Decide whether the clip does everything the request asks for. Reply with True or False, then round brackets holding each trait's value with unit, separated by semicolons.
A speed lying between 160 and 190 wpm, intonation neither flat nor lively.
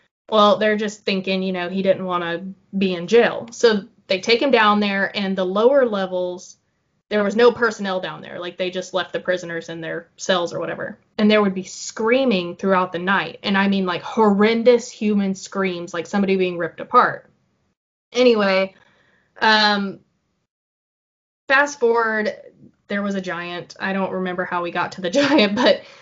True (180 wpm; 3.0 semitones)